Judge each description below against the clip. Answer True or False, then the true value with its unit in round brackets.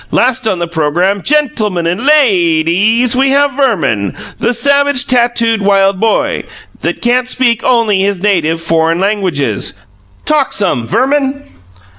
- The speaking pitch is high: True (215 Hz)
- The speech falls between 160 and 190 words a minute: False (145 wpm)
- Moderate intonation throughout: False (6.8 semitones)